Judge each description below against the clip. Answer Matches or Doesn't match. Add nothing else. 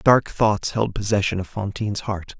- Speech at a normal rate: Matches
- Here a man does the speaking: Matches